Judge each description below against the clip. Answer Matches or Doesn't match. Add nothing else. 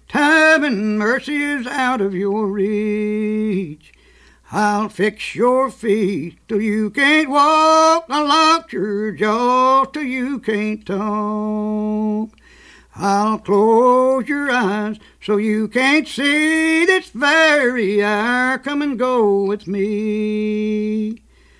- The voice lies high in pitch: Matches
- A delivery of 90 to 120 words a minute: Matches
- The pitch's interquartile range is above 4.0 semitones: Matches